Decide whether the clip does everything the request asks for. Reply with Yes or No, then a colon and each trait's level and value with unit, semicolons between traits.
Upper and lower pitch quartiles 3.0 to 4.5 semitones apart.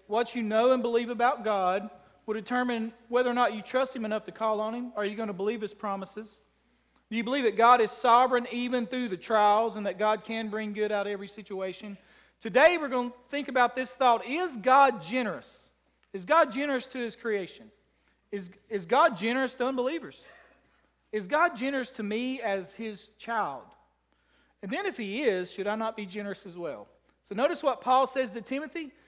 Yes: average, 3.4 semitones